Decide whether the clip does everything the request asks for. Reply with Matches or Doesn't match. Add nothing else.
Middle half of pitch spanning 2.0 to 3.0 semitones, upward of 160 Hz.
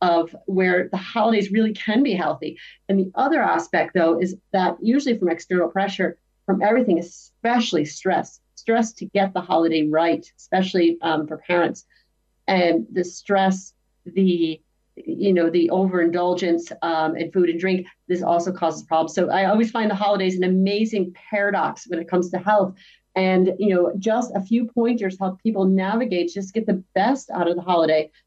Matches